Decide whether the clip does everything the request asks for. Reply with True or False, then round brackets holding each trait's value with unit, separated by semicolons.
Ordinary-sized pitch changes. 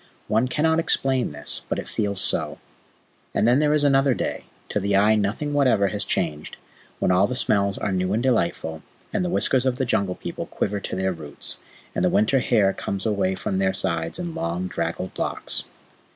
False (5.7 semitones)